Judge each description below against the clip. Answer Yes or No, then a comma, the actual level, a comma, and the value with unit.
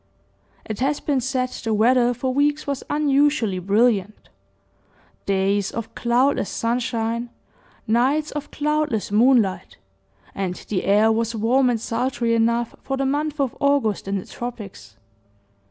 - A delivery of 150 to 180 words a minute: No, slow, 135 wpm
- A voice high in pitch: Yes, high, 240 Hz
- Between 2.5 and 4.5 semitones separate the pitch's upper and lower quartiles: Yes, average, 3.9 semitones